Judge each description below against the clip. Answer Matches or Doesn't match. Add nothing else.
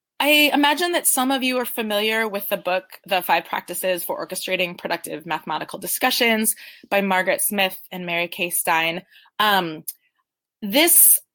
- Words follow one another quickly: Doesn't match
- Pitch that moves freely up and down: Matches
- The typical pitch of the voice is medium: Doesn't match